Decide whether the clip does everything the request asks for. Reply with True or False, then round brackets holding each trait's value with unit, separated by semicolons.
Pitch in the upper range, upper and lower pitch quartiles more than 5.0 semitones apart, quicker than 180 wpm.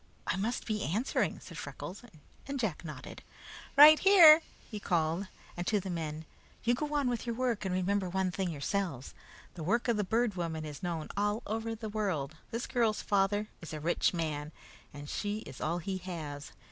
True (195 Hz; 5.4 semitones; 190 wpm)